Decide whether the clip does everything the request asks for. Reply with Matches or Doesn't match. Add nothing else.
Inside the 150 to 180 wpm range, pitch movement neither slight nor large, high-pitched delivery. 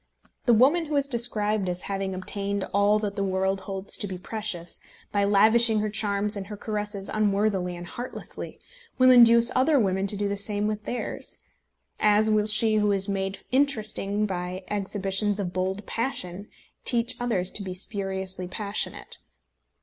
Doesn't match